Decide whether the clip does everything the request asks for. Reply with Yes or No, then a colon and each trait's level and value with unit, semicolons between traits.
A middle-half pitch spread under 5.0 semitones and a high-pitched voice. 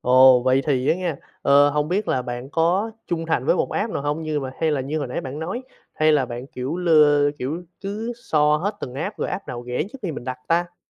No: average, 4.6 semitones; medium, 150 Hz